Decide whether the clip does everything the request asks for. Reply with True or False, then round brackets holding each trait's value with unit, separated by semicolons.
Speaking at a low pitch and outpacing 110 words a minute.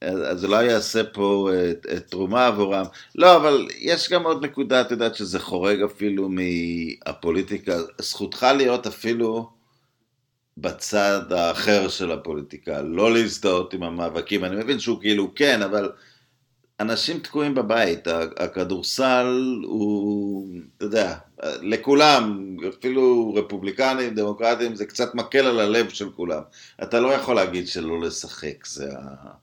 True (110 Hz; 130 wpm)